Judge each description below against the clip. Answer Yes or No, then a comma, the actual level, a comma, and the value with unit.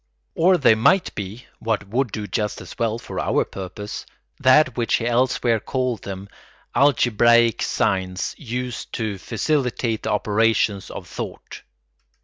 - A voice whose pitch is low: Yes, low, 115 Hz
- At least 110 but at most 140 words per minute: Yes, slow, 135 wpm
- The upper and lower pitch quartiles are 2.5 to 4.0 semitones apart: Yes, average, 3.3 semitones